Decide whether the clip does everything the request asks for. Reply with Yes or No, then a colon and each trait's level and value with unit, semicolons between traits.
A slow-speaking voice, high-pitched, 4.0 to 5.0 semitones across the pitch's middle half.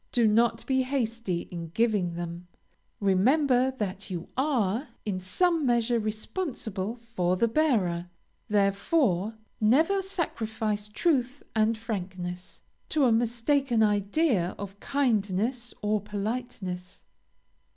Yes: slow, 110 wpm; high, 220 Hz; average, 4.6 semitones